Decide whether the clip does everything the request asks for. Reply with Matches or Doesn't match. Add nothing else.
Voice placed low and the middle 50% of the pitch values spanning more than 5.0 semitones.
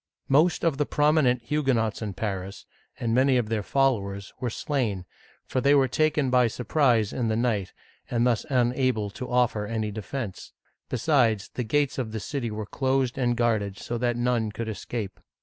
Doesn't match